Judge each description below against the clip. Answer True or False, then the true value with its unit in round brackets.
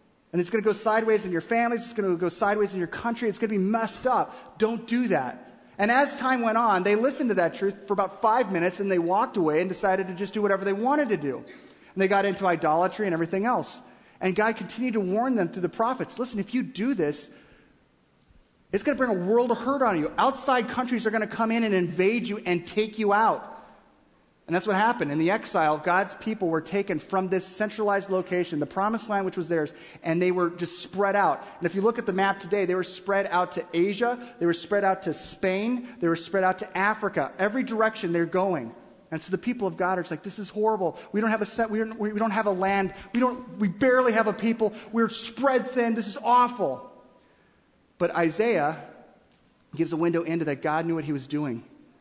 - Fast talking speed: True (235 wpm)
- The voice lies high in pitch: True (200 Hz)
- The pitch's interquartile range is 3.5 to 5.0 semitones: True (4.0 semitones)